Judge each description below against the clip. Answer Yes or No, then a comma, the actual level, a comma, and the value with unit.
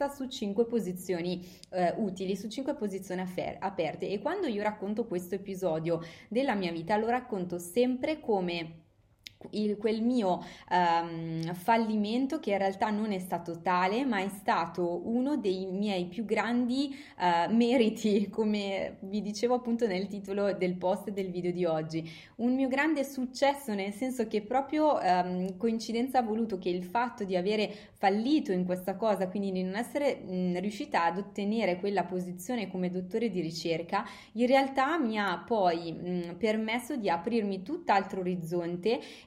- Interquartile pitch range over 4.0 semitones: Yes, average, 4.5 semitones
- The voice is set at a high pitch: Yes, high, 200 Hz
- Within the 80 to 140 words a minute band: No, average, 155 wpm